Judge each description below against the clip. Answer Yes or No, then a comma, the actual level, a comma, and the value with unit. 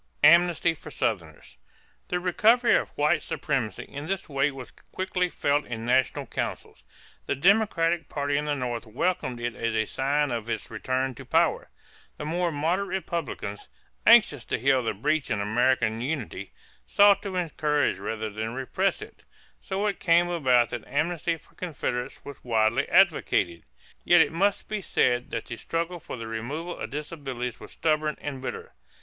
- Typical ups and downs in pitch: No, wide, 5.9 semitones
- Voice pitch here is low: No, medium, 145 Hz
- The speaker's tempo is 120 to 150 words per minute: No, average, 165 wpm